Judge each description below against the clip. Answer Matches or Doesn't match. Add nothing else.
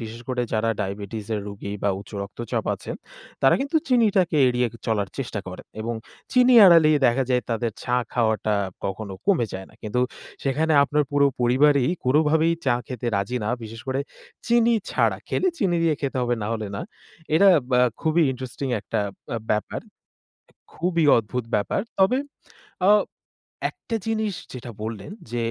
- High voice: Doesn't match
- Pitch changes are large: Matches